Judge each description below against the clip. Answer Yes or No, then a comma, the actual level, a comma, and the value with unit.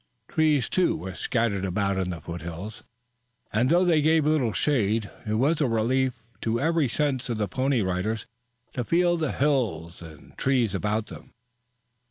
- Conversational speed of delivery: Yes, average, 165 wpm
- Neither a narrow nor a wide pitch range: No, wide, 6.6 semitones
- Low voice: Yes, low, 115 Hz